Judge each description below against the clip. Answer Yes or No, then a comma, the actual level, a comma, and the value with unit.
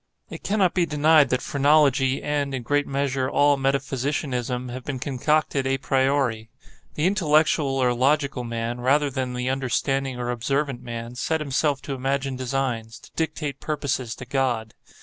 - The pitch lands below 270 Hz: Yes, low, 135 Hz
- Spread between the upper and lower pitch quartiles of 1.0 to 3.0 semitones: Yes, narrow, 2.5 semitones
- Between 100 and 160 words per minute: Yes, average, 150 wpm